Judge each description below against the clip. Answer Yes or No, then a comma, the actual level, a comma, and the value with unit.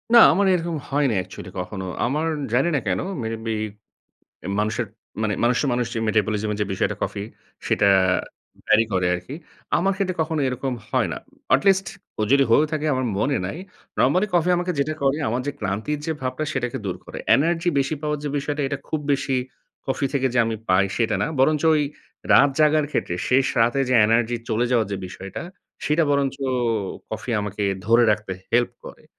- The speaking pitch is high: No, low, 130 Hz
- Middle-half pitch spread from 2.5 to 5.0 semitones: No, wide, 5.4 semitones